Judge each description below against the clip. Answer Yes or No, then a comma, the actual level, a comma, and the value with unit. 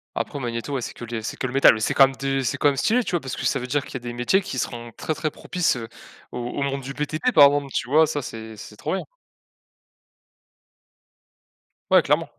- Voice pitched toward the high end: No, low, 135 Hz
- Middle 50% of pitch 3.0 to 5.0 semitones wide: Yes, average, 3.4 semitones